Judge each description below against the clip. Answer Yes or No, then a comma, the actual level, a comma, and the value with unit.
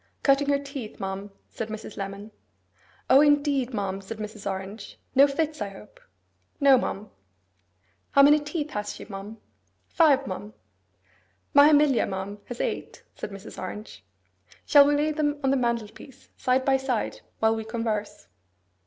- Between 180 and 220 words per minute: No, average, 155 wpm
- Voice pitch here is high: Yes, high, 235 Hz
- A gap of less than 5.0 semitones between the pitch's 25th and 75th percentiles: No, wide, 5.4 semitones